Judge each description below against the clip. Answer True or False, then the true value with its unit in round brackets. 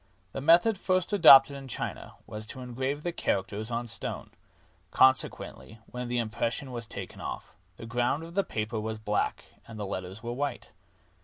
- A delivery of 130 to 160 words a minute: False (170 wpm)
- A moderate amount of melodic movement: True (4.3 semitones)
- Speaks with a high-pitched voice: False (120 Hz)